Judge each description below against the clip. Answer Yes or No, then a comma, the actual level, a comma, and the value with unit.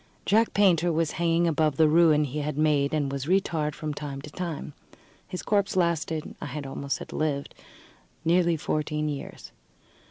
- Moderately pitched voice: Yes, medium, 155 Hz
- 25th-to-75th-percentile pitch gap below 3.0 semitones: Yes, narrow, 2.4 semitones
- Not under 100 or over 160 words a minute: No, average, 170 wpm